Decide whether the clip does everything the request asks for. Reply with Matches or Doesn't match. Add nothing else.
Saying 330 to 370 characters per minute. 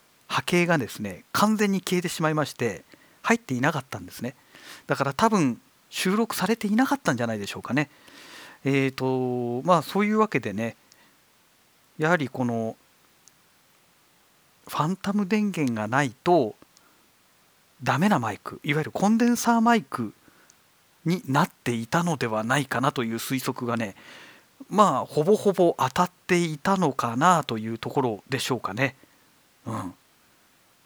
Doesn't match